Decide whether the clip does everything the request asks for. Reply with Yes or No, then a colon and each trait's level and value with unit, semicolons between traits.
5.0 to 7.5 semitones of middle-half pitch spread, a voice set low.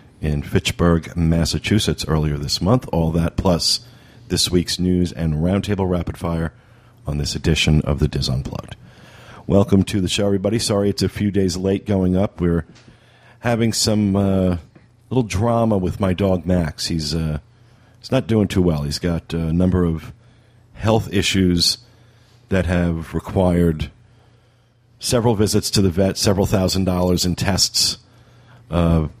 Yes: average, 5.3 semitones; very low, 95 Hz